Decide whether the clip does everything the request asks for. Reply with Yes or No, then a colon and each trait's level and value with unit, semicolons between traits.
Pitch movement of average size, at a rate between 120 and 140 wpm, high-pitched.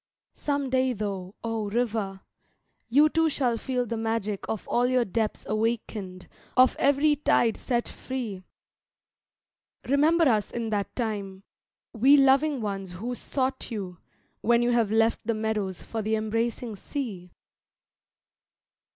Yes: average, 3.6 semitones; slow, 135 wpm; high, 230 Hz